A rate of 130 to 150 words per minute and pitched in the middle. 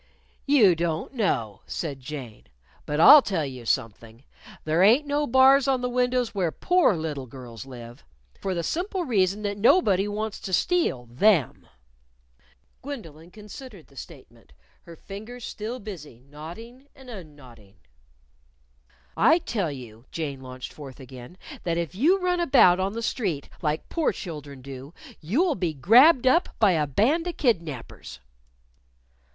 Yes: average, 145 wpm; medium, 180 Hz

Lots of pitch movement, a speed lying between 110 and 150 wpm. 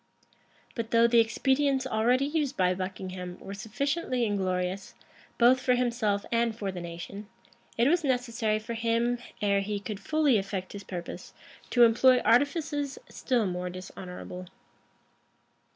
No: average, 4.6 semitones; slow, 135 wpm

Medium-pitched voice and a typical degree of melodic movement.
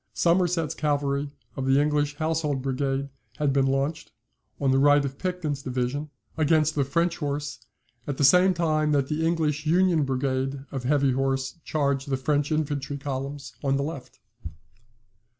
No: medium, 145 Hz; narrow, 2.2 semitones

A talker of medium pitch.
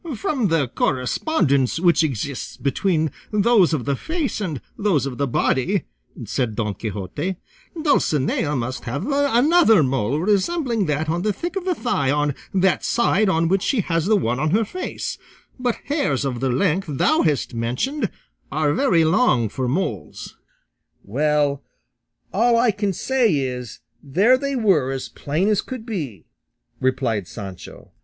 Yes: medium, 160 Hz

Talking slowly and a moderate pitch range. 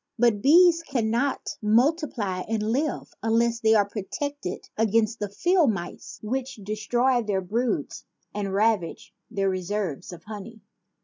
Yes: slow, 130 wpm; average, 3.5 semitones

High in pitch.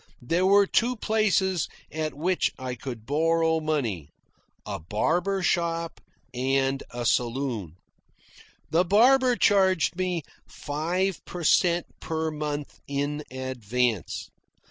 No: medium, 155 Hz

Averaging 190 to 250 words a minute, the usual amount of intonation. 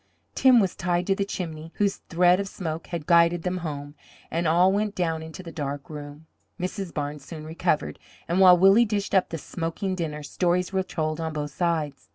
Yes: average, 200 wpm; average, 3.1 semitones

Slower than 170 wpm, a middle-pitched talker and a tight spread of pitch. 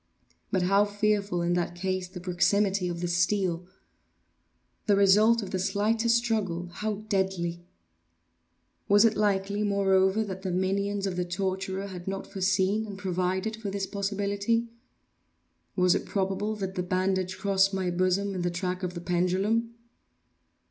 No: average, 150 wpm; high, 195 Hz; narrow, 2.0 semitones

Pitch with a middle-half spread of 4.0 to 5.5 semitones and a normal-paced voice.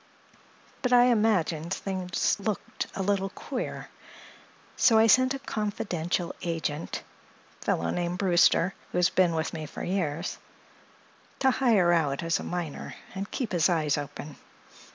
No: average, 4.3 semitones; slow, 130 wpm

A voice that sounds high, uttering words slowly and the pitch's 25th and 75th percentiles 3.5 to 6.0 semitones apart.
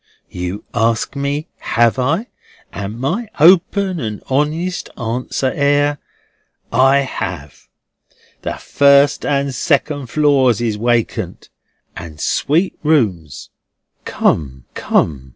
No: low, 135 Hz; slow, 105 wpm; average, 4.6 semitones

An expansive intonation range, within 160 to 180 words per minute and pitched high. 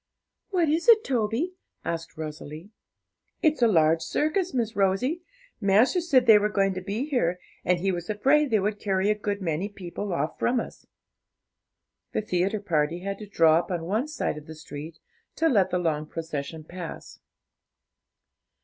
Yes: wide, 6.1 semitones; average, 170 wpm; high, 195 Hz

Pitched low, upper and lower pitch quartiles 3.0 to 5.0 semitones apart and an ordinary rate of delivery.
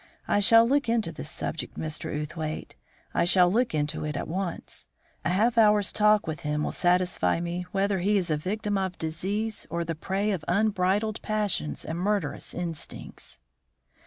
No: medium, 185 Hz; average, 4.1 semitones; average, 170 wpm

